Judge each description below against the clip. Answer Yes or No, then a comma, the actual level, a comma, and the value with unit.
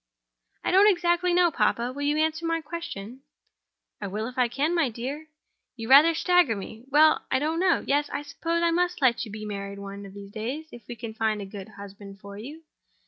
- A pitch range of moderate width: No, wide, 7.4 semitones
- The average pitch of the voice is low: No, very high, 265 Hz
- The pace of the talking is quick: Yes, fast, 210 wpm